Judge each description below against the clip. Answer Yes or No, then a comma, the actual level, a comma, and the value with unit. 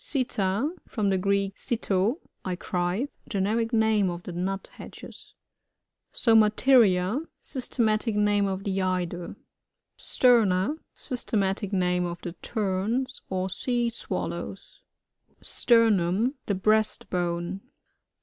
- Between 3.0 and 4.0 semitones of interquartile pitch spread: Yes, average, 3.7 semitones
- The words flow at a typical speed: No, slow, 105 wpm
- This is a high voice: Yes, high, 200 Hz